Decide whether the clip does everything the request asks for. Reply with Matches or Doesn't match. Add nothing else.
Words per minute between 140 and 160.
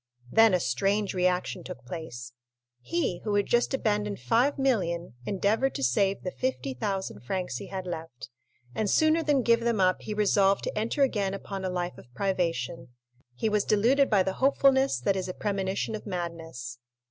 Doesn't match